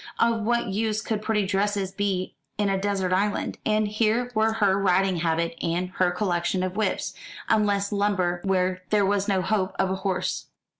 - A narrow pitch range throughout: Yes, narrow, 2.3 semitones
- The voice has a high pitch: Yes, high, 200 Hz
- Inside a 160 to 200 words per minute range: Yes, average, 180 wpm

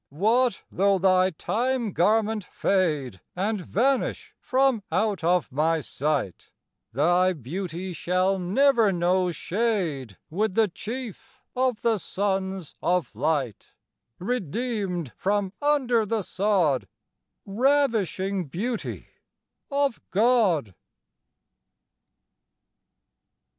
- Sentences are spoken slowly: Yes, slow, 90 wpm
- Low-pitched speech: No, high, 195 Hz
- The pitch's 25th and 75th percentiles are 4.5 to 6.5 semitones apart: Yes, average, 4.8 semitones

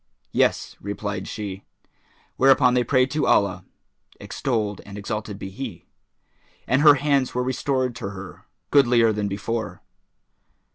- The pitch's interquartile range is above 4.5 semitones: No, average, 4.2 semitones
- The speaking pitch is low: Yes, low, 115 Hz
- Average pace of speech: No, slow, 130 wpm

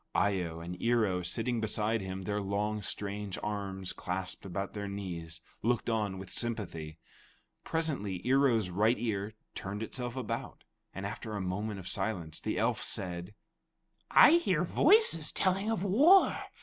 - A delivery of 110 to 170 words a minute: Yes, average, 150 wpm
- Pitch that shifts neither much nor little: Yes, average, 3.9 semitones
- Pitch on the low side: Yes, low, 105 Hz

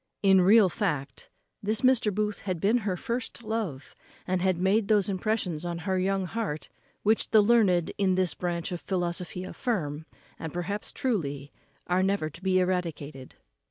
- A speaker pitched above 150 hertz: Yes, medium, 185 Hz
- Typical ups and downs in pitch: Yes, average, 3.5 semitones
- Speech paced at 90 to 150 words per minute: No, average, 160 wpm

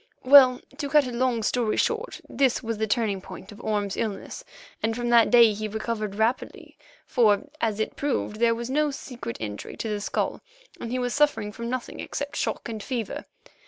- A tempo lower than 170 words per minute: No, average, 195 wpm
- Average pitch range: Yes, average, 3.0 semitones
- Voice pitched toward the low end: No, high, 230 Hz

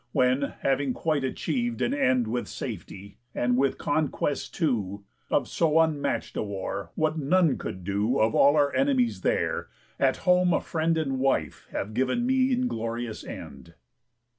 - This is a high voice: No, medium, 140 Hz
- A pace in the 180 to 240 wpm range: No, average, 155 wpm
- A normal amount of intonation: No, wide, 6.1 semitones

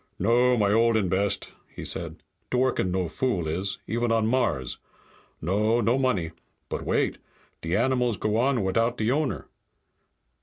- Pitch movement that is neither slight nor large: Yes, average, 4.1 semitones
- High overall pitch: No, low, 115 Hz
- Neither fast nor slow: Yes, average, 150 wpm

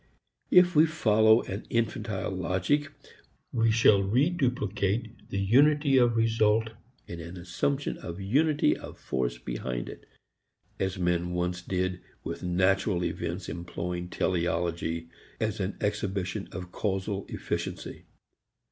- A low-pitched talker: Yes, very low, 95 Hz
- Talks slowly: Yes, slow, 120 wpm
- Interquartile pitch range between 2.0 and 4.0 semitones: No, average, 4.4 semitones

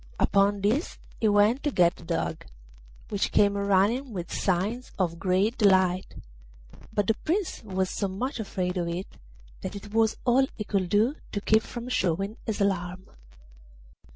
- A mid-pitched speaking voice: No, high, 200 Hz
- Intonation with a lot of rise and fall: No, average, 3.1 semitones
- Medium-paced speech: Yes, average, 160 wpm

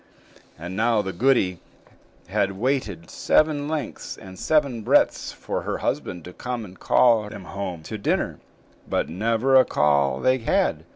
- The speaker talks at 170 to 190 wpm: No, average, 155 wpm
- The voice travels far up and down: Yes, wide, 5.9 semitones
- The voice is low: Yes, low, 105 Hz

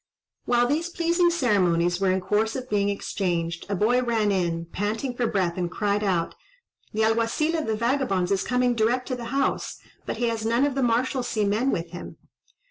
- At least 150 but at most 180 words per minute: No, average, 195 wpm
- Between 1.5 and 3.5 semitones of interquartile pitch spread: No, average, 4.6 semitones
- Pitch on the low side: No, high, 220 Hz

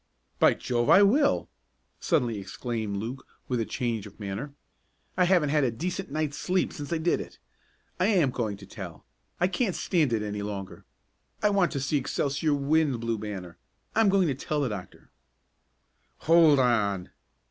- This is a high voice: No, low, 135 Hz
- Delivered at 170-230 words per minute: Yes, average, 175 wpm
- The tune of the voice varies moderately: No, wide, 7.6 semitones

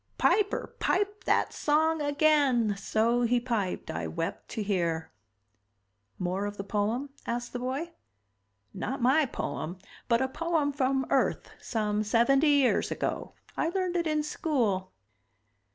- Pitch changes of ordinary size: No, wide, 6.3 semitones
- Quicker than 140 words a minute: No, slow, 135 wpm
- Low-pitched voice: No, very high, 250 Hz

